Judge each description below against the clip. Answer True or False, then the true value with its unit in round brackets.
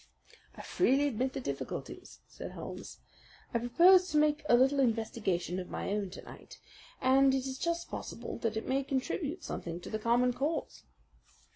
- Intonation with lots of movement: False (4.2 semitones)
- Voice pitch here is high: True (260 Hz)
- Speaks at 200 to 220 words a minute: False (170 wpm)